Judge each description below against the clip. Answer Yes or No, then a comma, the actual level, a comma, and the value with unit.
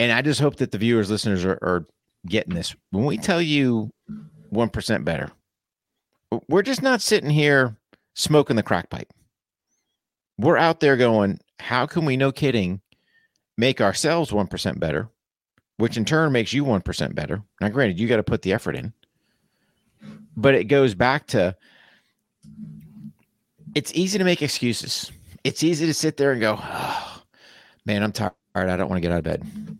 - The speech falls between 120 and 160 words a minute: No, average, 175 wpm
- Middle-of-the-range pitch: No, low, 125 Hz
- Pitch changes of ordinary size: No, wide, 6.7 semitones